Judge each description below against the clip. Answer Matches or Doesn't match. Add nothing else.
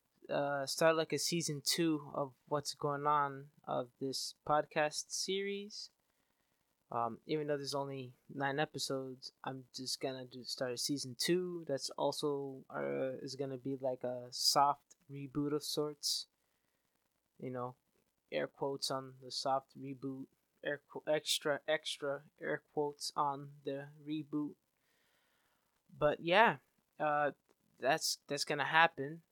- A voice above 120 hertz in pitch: Matches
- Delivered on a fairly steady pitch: Matches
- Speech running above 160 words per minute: Doesn't match